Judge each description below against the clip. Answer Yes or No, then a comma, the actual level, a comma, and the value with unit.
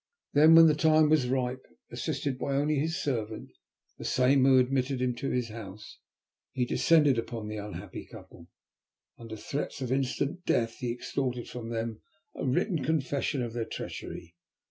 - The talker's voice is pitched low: Yes, low, 130 Hz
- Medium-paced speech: Yes, average, 165 wpm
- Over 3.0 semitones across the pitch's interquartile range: Yes, average, 3.6 semitones